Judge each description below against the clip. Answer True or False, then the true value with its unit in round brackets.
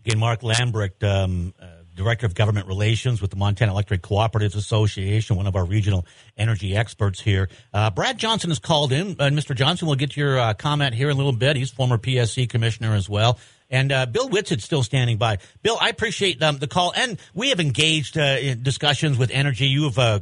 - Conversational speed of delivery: False (220 wpm)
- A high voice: False (120 Hz)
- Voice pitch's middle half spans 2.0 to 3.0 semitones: False (5.3 semitones)